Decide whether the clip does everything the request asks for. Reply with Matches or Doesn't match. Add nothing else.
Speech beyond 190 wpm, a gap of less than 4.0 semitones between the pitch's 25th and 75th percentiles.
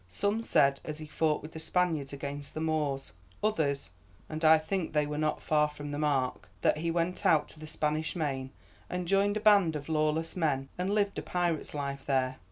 Matches